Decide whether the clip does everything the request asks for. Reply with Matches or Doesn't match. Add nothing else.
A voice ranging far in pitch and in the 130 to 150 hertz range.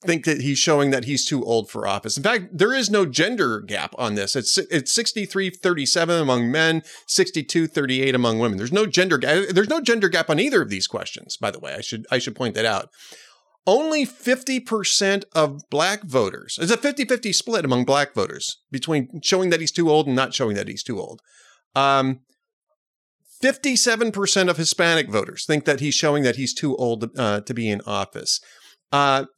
Doesn't match